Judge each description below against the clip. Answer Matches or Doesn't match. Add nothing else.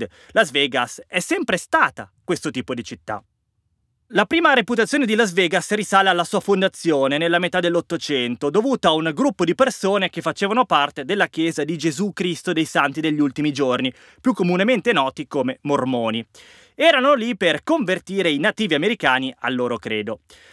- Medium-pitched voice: Matches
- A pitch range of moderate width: Doesn't match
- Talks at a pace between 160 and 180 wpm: Matches